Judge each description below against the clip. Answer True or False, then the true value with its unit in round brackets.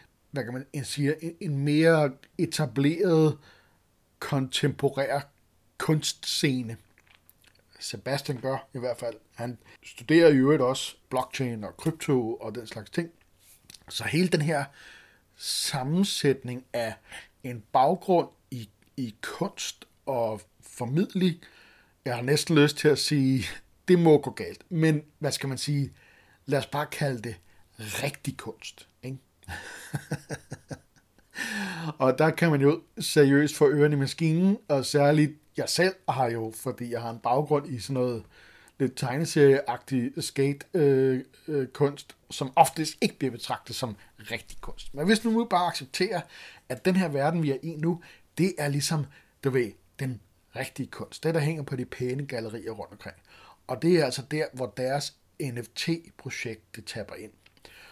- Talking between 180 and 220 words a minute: False (145 wpm)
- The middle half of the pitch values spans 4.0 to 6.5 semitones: True (4.4 semitones)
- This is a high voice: False (135 Hz)